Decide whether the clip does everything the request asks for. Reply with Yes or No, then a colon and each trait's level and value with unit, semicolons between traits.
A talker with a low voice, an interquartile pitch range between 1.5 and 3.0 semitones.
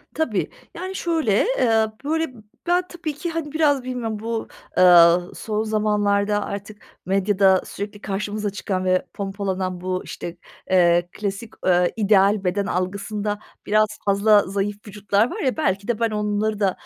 No: high, 205 Hz; narrow, 2.5 semitones